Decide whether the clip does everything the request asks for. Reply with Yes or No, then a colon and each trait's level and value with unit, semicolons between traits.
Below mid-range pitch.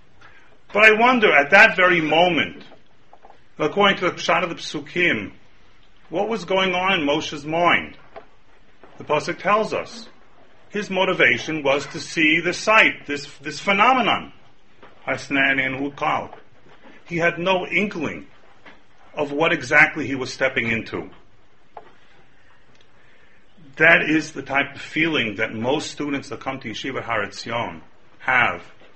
No: medium, 155 Hz